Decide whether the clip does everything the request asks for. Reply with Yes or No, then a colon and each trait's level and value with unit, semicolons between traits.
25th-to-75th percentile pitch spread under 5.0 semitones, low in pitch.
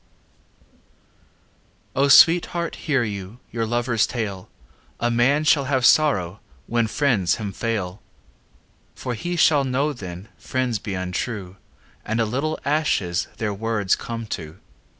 No: wide, 5.5 semitones; low, 115 Hz